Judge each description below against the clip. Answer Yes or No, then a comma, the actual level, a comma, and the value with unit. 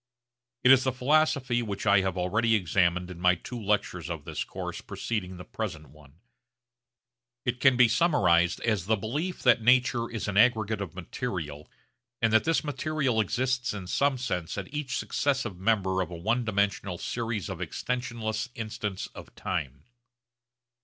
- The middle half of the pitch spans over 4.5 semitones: Yes, average, 5.1 semitones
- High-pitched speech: No, low, 110 Hz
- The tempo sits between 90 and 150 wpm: No, average, 160 wpm